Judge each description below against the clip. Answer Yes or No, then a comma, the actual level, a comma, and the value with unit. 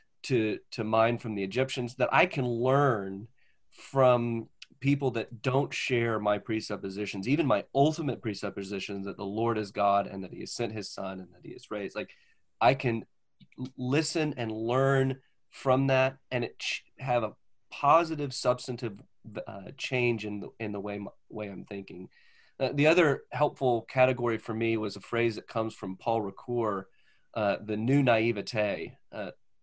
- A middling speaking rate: Yes, average, 170 wpm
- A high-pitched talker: No, low, 115 Hz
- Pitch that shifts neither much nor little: Yes, average, 4.1 semitones